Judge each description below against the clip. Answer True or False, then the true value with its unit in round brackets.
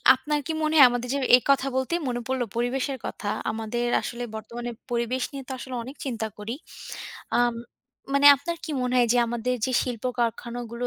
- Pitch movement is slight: True (1.8 semitones)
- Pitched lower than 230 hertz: False (245 Hz)